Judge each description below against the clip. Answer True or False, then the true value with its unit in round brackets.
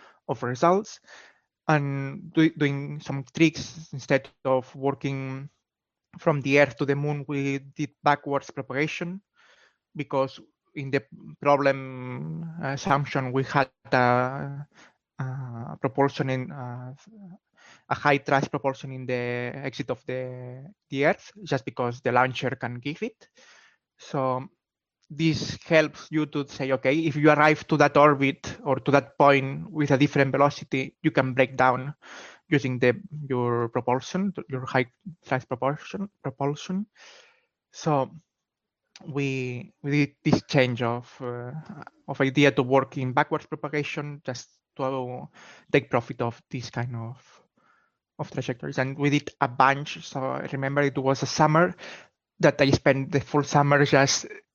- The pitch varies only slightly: True (2.3 semitones)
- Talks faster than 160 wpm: False (140 wpm)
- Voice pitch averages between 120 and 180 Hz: True (140 Hz)